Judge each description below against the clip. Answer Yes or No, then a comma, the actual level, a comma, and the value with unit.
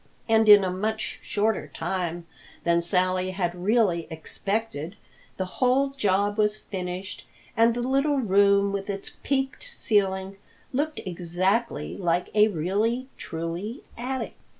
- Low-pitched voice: No, high, 200 Hz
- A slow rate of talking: Yes, slow, 125 wpm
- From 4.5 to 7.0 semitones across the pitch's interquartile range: No, average, 3.9 semitones